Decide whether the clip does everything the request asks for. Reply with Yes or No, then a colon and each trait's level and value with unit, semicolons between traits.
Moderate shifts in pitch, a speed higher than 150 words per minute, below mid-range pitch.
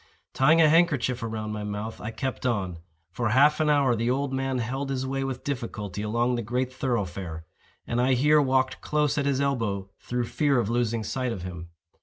Yes: average, 3.9 semitones; average, 200 wpm; low, 125 Hz